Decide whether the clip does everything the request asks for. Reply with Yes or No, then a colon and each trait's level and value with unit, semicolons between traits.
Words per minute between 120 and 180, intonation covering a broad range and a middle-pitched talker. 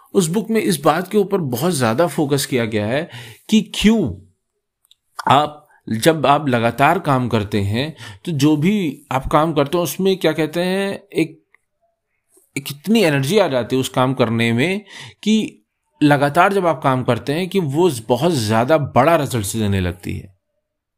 Yes: average, 170 wpm; wide, 6.7 semitones; medium, 145 Hz